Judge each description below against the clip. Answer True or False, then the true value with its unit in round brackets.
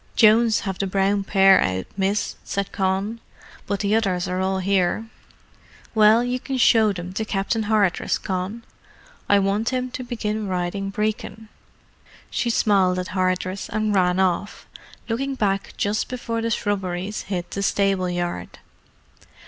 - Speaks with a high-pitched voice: True (200 Hz)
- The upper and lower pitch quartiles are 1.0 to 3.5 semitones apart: True (2.7 semitones)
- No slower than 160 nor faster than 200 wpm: False (150 wpm)